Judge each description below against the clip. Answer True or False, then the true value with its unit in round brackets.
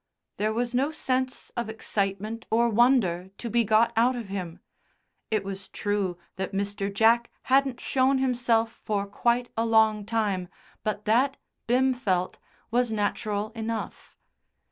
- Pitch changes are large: False (3.1 semitones)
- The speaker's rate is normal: True (145 wpm)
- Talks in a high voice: True (225 Hz)